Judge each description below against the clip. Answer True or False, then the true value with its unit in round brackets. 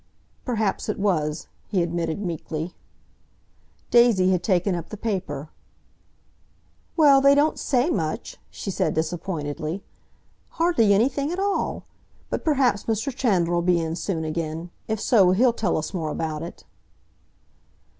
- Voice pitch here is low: False (185 Hz)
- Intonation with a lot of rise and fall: True (6.3 semitones)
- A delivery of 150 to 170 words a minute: False (135 wpm)